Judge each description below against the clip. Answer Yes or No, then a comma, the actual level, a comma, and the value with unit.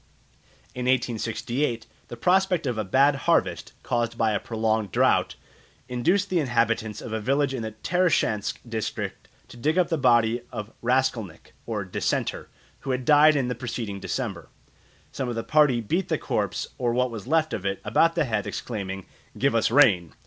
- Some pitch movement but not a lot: Yes, average, 4.1 semitones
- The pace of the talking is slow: No, average, 180 wpm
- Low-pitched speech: Yes, low, 120 Hz